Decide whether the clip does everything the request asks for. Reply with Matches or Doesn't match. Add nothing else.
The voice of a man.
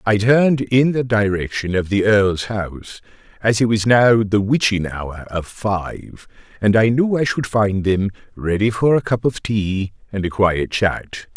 Matches